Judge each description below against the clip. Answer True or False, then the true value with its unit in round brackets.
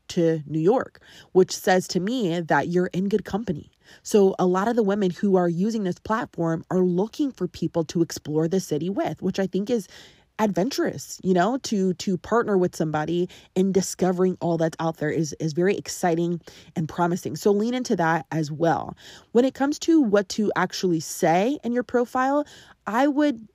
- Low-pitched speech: False (185 Hz)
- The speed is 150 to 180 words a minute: False (190 wpm)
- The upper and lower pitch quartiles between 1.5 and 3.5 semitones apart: False (4.2 semitones)